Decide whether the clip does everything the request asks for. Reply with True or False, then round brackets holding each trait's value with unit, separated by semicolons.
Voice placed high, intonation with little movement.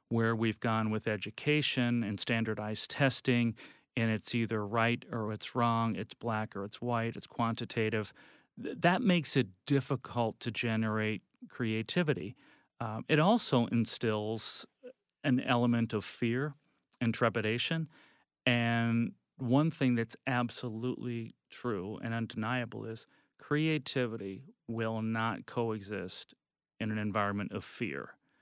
False (115 Hz; 2.3 semitones)